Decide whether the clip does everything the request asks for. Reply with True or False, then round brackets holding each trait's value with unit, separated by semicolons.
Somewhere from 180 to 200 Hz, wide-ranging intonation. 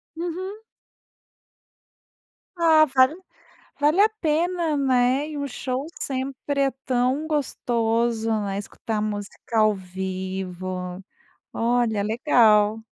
False (245 Hz; 5.7 semitones)